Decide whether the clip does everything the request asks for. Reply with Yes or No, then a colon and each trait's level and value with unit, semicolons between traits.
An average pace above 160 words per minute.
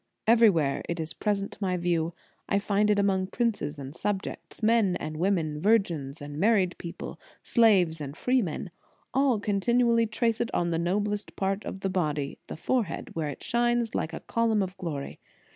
Yes: average, 175 wpm